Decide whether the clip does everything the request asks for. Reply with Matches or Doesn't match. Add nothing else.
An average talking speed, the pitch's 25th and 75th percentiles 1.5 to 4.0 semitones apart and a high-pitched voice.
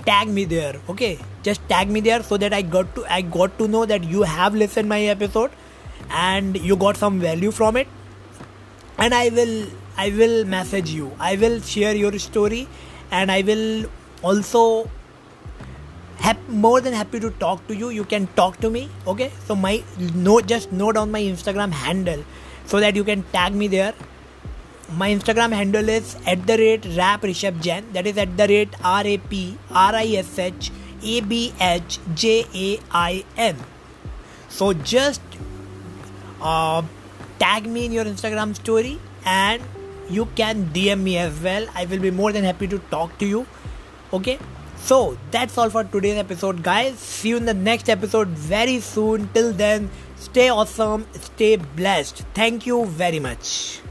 Matches